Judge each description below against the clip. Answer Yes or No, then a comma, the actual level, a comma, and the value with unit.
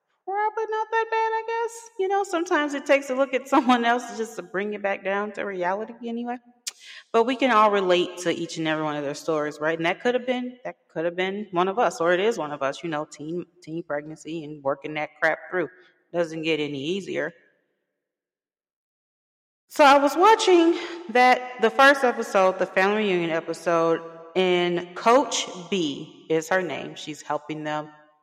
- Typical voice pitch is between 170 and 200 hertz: Yes, medium, 185 Hz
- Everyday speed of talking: Yes, average, 195 wpm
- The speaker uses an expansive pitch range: Yes, wide, 7.4 semitones